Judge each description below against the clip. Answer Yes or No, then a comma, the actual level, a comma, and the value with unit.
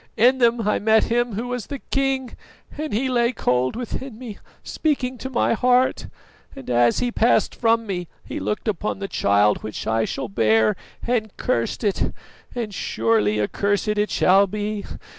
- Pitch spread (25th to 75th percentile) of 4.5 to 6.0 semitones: Yes, wide, 5.6 semitones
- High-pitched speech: Yes, high, 215 Hz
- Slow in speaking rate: No, average, 170 wpm